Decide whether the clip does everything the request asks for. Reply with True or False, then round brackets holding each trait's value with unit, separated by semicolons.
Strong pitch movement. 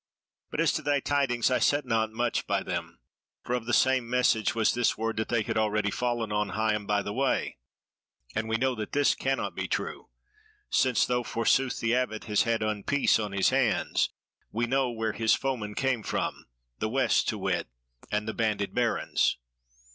False (2.8 semitones)